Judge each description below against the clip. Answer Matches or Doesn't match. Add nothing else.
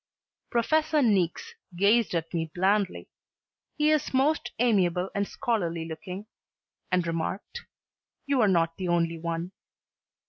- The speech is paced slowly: Matches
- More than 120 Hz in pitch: Matches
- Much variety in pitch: Matches